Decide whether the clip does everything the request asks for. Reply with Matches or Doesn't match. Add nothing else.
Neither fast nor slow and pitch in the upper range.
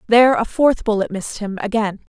Matches